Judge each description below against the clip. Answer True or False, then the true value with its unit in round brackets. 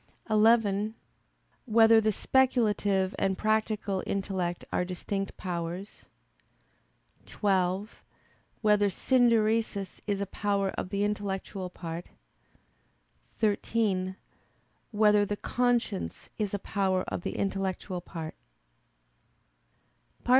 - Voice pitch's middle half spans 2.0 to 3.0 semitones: True (2.4 semitones)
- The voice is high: True (200 Hz)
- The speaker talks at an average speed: False (90 wpm)